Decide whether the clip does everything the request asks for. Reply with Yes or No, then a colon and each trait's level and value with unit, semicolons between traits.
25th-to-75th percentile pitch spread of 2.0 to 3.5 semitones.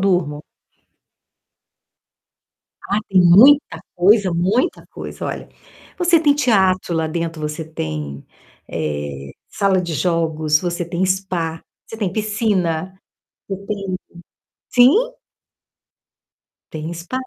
No: average, 3.9 semitones